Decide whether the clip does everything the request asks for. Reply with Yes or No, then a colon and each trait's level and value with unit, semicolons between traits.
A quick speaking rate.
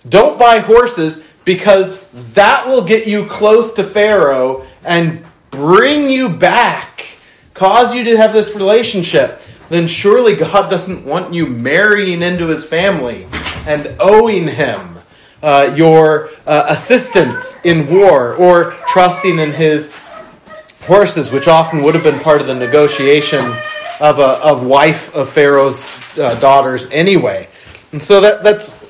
No: average, 140 wpm